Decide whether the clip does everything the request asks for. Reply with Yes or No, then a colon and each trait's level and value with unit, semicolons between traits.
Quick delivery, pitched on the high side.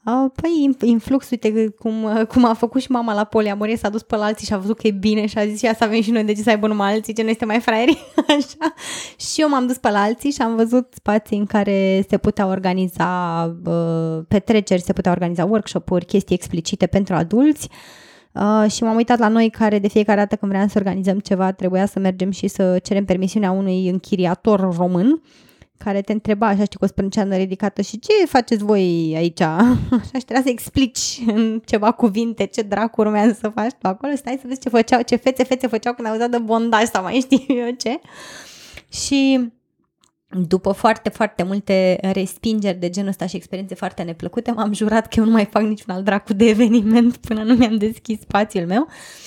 Yes: fast, 210 wpm; high, 215 Hz